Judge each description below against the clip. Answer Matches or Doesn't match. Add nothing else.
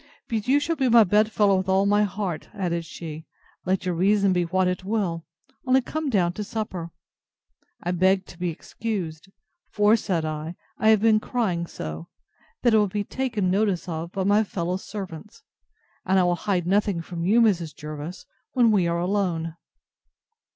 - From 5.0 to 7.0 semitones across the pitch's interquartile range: Doesn't match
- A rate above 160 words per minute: Matches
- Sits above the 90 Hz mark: Matches